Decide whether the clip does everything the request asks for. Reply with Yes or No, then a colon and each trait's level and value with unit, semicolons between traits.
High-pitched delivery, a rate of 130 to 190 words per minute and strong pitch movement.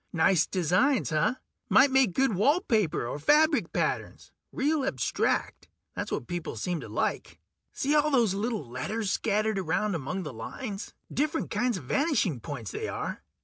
Yes: high, 210 Hz; average, 160 wpm; wide, 8.6 semitones